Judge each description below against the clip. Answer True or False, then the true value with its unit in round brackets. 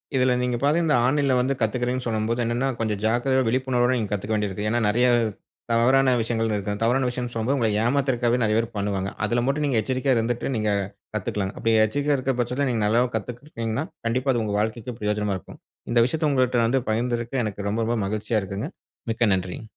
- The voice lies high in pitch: False (120 Hz)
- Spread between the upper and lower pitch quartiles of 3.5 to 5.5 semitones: False (2.9 semitones)